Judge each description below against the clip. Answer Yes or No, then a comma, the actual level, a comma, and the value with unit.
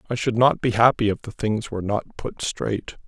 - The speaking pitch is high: No, low, 110 Hz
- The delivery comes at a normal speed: No, fast, 235 wpm